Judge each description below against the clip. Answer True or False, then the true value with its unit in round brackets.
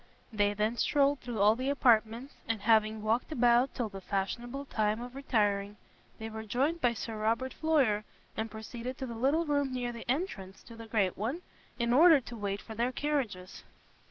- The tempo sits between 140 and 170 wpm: False (185 wpm)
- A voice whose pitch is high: True (235 Hz)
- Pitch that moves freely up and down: False (3.4 semitones)